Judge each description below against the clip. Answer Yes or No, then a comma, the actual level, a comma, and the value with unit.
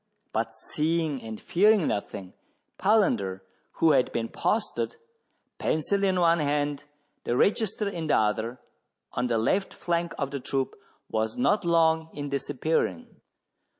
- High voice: No, medium, 150 Hz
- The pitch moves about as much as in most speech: No, wide, 6.4 semitones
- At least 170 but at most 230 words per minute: No, slow, 135 wpm